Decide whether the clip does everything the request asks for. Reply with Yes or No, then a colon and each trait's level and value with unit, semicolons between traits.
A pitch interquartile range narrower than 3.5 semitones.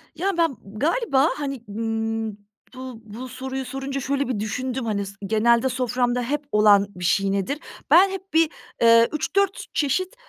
No: average, 4.4 semitones